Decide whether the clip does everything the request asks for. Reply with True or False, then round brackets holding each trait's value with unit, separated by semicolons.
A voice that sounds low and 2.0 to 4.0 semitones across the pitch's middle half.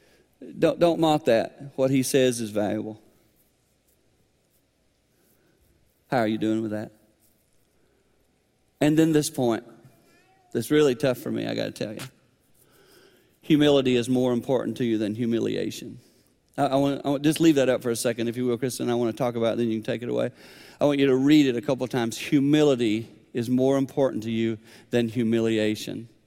True (120 Hz; 3.5 semitones)